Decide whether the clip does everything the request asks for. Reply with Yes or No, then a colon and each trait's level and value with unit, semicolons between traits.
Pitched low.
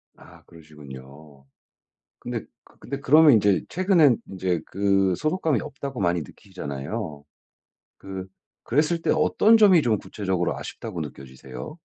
Yes: very low, 95 Hz